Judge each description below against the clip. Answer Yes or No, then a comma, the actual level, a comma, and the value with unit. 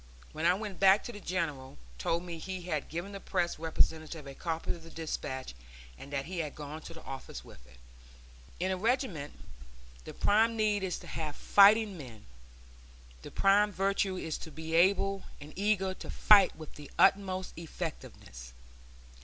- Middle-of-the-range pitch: Yes, medium, 175 Hz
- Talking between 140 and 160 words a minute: No, average, 170 wpm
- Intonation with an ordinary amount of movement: Yes, average, 4.0 semitones